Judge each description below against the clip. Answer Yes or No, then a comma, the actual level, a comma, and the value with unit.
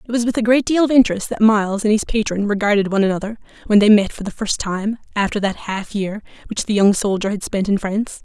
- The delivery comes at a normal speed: No, fast, 255 wpm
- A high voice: Yes, high, 210 Hz